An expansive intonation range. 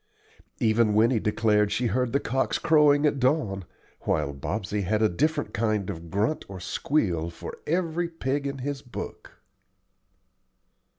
Yes: wide, 6.1 semitones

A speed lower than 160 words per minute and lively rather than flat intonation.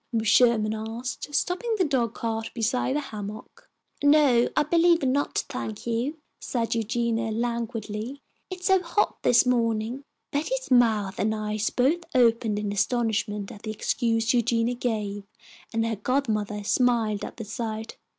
No: average, 145 wpm; average, 2.9 semitones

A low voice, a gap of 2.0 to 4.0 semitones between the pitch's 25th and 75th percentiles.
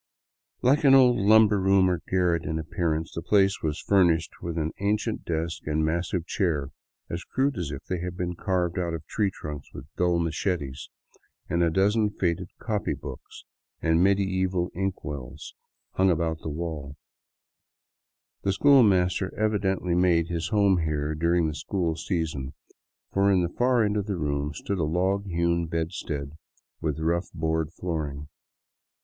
Yes: very low, 85 Hz; average, 3.3 semitones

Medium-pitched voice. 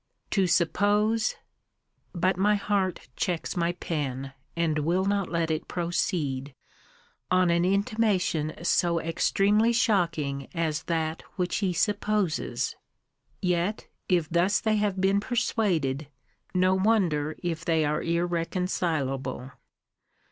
Yes: medium, 175 Hz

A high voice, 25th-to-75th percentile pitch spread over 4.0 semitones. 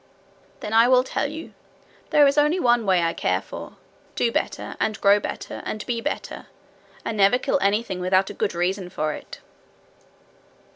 Yes: high, 215 Hz; average, 4.9 semitones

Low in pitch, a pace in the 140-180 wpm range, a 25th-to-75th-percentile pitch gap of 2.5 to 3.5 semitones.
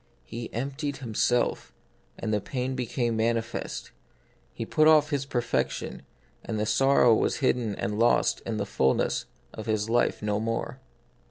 Yes: low, 115 Hz; average, 155 wpm; average, 3.1 semitones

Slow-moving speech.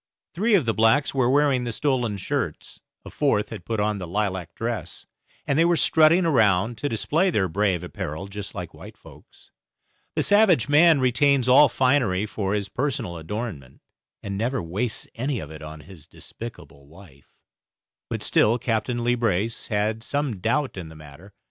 No: average, 175 wpm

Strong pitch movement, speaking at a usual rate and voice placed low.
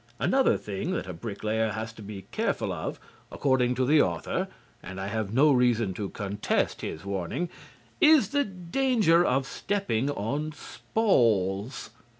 Yes: wide, 8.2 semitones; average, 150 wpm; low, 120 Hz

